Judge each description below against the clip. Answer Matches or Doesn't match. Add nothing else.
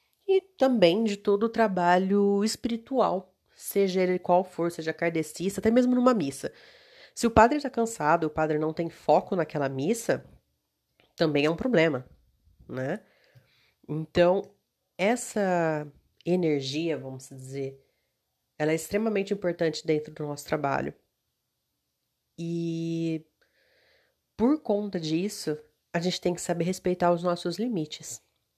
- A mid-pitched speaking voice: Matches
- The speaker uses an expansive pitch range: Doesn't match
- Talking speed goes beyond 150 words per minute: Doesn't match